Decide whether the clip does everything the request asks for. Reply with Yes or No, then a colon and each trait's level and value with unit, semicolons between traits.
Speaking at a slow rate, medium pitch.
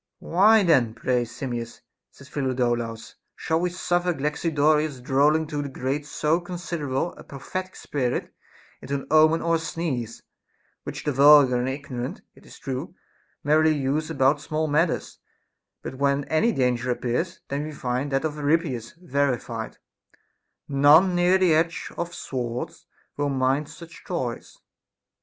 No: average, 145 wpm; medium, 145 Hz